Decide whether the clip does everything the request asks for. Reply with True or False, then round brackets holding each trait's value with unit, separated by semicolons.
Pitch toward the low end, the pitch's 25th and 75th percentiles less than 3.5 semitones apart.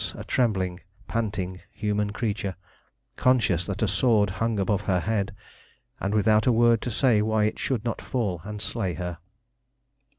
True (105 Hz; 3.0 semitones)